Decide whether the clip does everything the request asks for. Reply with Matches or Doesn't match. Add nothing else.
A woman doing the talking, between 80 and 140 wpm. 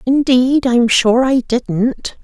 Matches